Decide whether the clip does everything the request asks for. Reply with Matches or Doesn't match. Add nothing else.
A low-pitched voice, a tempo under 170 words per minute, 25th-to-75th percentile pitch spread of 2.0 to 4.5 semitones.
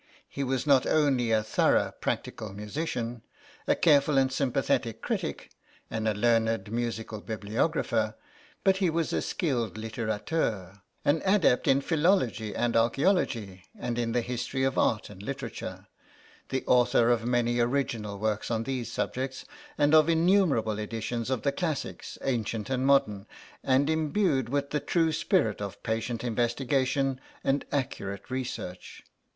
Matches